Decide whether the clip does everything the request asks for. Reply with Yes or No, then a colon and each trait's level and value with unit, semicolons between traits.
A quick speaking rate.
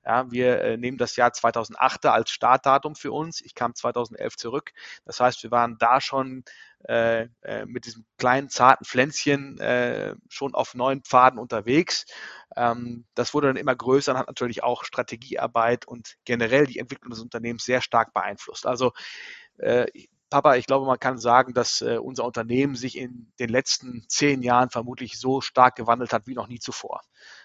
No: average, 175 wpm